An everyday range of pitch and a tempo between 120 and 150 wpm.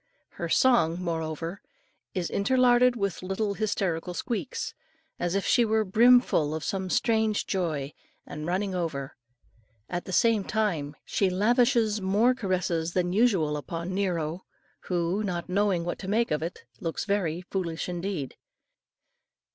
Yes: average, 4.1 semitones; average, 140 wpm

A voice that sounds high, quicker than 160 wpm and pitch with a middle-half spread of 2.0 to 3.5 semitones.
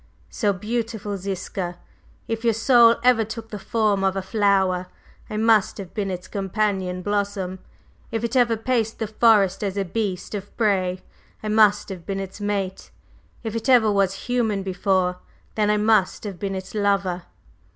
Yes: high, 205 Hz; average, 170 wpm; narrow, 2.6 semitones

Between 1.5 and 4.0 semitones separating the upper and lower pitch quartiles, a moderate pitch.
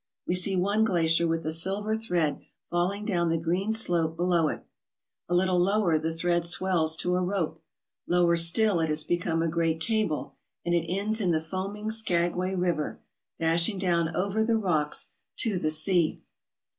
Yes: average, 3.0 semitones; medium, 175 Hz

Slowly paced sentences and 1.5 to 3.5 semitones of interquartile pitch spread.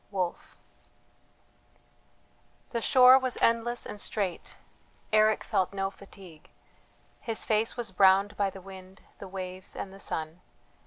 Yes: slow, 125 wpm; average, 2.8 semitones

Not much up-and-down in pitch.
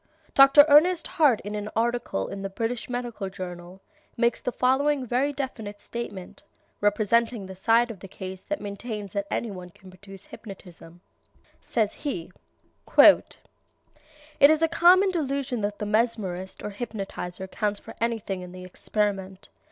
No: average, 4.3 semitones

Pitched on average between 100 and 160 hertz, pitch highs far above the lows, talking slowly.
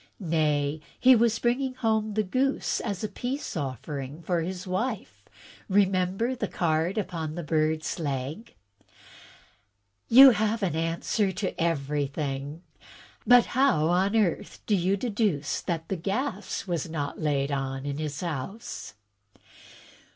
No: medium, 175 Hz; wide, 6.1 semitones; slow, 130 wpm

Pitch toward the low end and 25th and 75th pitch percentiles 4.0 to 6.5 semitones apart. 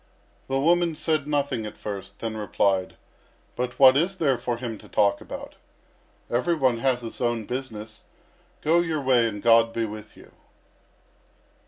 Yes: low, 120 Hz; average, 4.4 semitones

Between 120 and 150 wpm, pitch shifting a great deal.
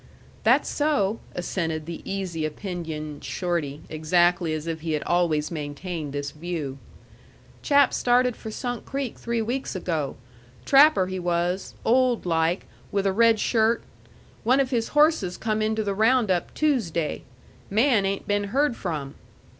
Yes: average, 145 wpm; wide, 6.2 semitones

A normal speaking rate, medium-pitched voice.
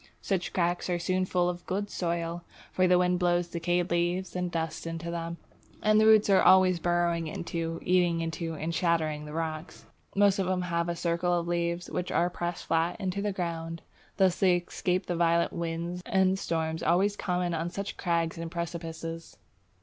Yes: average, 185 wpm; medium, 175 Hz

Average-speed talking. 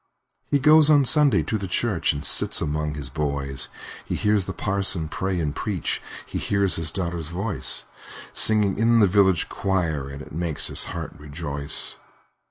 Yes: average, 170 wpm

